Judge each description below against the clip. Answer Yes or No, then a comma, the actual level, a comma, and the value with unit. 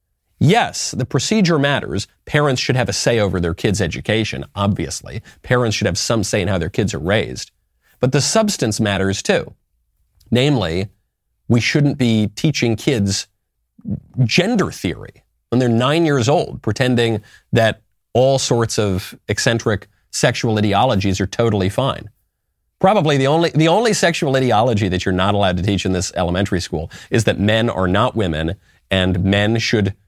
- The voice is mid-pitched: No, low, 110 Hz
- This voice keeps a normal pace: Yes, average, 160 wpm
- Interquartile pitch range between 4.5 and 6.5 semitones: Yes, average, 4.8 semitones